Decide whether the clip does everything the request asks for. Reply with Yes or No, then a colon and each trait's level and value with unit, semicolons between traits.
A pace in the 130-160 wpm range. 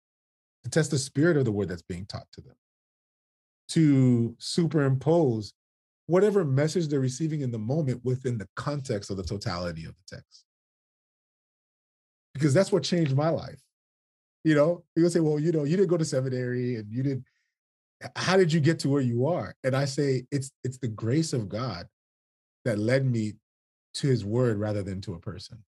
No: average, 185 wpm